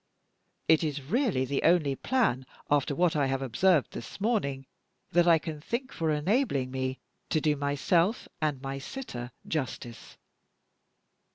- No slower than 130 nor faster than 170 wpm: Yes, average, 150 wpm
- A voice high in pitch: No, medium, 150 Hz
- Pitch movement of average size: Yes, average, 4.7 semitones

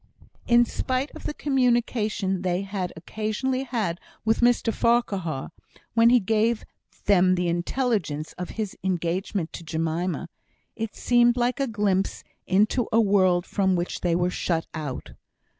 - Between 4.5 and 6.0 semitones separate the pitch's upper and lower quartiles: Yes, average, 5.1 semitones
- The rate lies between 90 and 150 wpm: Yes, average, 140 wpm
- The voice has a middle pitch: No, high, 200 Hz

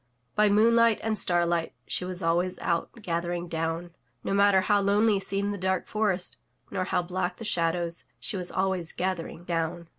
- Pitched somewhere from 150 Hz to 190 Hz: Yes, medium, 185 Hz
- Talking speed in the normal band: Yes, average, 170 wpm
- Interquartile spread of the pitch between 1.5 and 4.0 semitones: Yes, average, 2.7 semitones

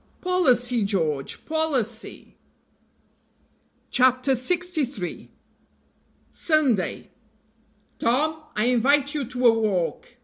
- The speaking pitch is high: Yes, very high, 250 Hz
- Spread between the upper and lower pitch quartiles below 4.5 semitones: No, average, 5.1 semitones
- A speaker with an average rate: No, slow, 75 wpm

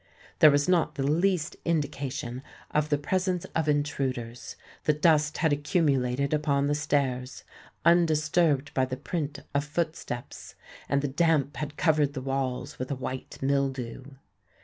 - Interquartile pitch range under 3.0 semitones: Yes, narrow, 2.5 semitones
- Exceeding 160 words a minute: No, average, 145 wpm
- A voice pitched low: No, medium, 145 Hz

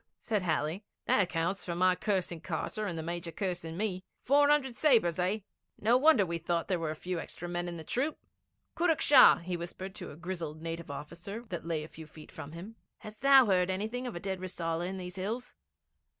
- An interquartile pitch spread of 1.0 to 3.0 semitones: No, average, 4.1 semitones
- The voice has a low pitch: No, medium, 180 Hz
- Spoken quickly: Yes, fast, 215 wpm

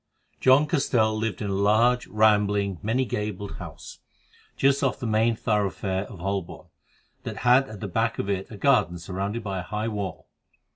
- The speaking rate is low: No, average, 175 wpm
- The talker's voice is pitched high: No, low, 105 Hz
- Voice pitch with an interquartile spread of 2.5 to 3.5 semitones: Yes, average, 3.0 semitones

